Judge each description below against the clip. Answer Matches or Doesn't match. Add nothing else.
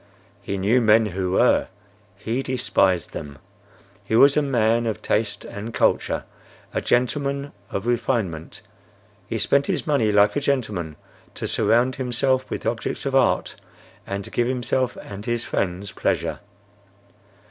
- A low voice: Matches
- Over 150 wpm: Doesn't match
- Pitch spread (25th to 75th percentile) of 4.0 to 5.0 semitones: Matches